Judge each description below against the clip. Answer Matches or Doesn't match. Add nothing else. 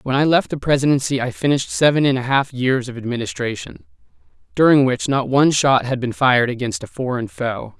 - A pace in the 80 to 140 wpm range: Doesn't match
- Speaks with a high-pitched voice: Doesn't match